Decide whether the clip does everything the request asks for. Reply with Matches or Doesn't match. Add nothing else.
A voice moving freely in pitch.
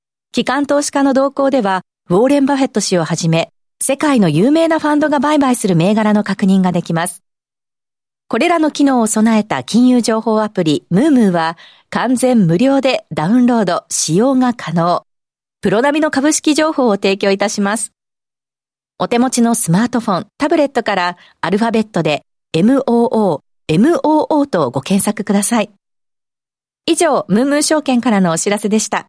Matches